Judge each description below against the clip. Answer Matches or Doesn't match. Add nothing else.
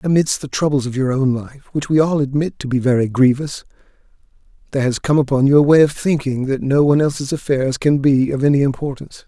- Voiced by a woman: Doesn't match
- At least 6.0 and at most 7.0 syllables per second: Matches